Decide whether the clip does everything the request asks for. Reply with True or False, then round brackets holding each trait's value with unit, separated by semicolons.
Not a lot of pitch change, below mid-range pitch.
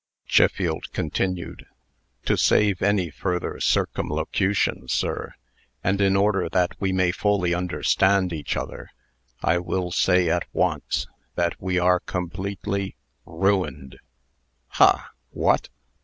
True (1.9 semitones; 90 Hz)